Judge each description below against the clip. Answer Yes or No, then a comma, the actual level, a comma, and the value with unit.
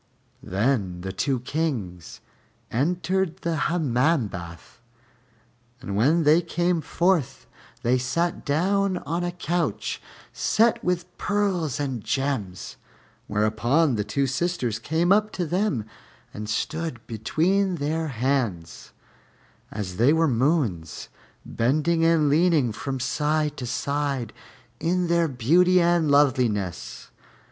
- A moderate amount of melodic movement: No, wide, 6.5 semitones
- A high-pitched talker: No, medium, 145 Hz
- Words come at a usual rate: No, slow, 115 wpm